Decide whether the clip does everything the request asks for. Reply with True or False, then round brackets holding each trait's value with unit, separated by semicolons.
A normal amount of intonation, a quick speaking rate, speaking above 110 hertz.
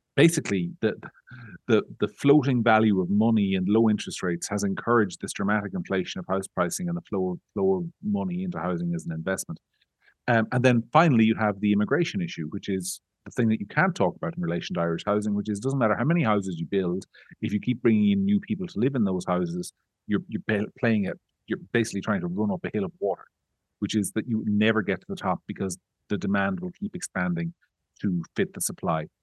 False (5.0 semitones; 225 wpm; 105 Hz)